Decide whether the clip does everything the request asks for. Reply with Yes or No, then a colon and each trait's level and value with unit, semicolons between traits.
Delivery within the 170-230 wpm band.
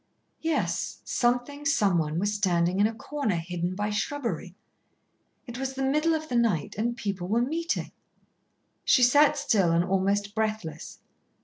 No: average, 145 wpm